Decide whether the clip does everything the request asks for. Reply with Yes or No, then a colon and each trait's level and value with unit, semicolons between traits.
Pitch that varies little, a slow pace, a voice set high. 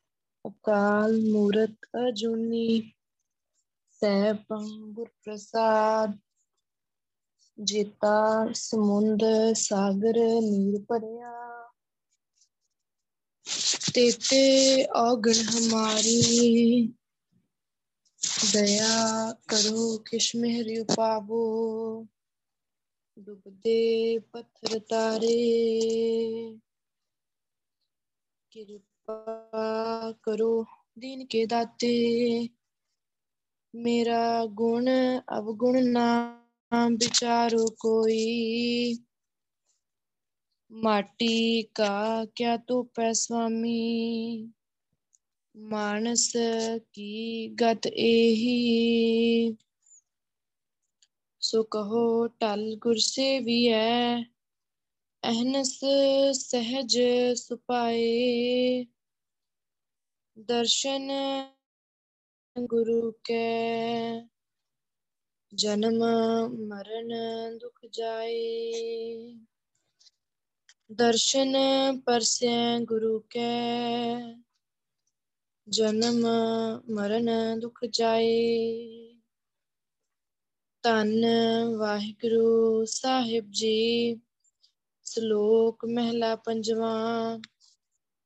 Yes: narrow, 1.0 semitones; slow, 50 wpm; high, 230 Hz